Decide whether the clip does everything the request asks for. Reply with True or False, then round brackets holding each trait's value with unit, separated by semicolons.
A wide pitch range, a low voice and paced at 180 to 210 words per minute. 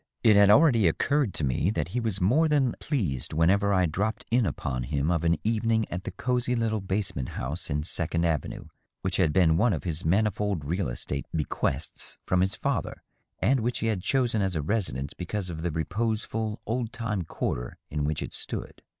True (5.8 semitones; 95 Hz; 195 wpm)